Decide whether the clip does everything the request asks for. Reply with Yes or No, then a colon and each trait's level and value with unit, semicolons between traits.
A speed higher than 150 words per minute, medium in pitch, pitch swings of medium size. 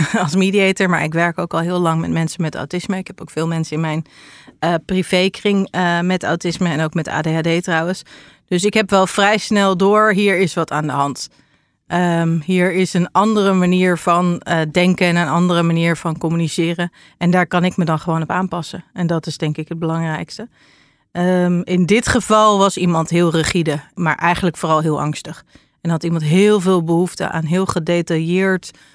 No: average, 200 wpm; medium, 175 Hz; narrow, 2.3 semitones